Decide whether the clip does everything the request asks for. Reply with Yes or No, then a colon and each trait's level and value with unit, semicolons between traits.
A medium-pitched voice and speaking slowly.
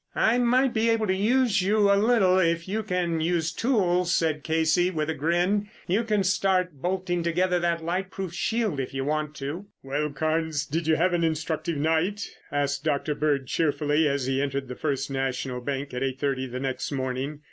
No: medium, 165 Hz; average, 195 wpm